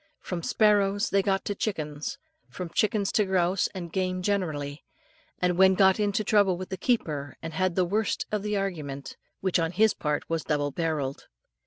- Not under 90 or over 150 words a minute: No, average, 180 wpm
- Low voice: No, medium, 185 Hz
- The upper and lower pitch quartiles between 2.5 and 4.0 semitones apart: Yes, average, 3.7 semitones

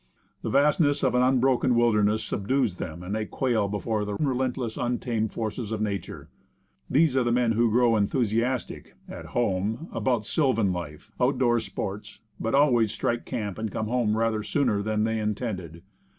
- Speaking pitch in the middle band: No, low, 115 Hz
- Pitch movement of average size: Yes, average, 3.0 semitones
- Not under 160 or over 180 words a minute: Yes, average, 170 wpm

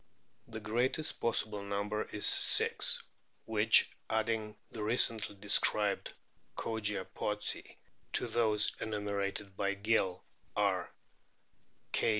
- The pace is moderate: No, slow, 100 wpm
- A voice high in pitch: No, low, 105 Hz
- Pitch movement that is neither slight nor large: No, narrow, 1.7 semitones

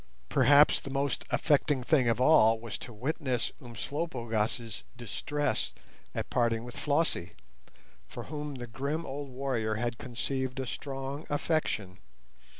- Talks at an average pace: No, slow, 130 wpm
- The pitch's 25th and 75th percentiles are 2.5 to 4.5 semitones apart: Yes, average, 3.7 semitones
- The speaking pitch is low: Yes, low, 130 Hz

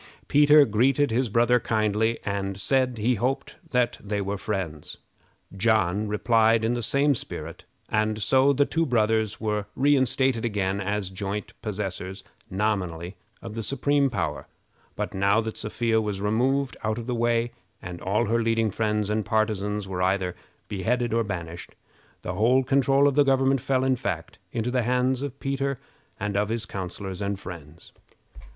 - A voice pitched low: Yes, low, 110 Hz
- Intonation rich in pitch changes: No, average, 3.8 semitones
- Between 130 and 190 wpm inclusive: Yes, average, 160 wpm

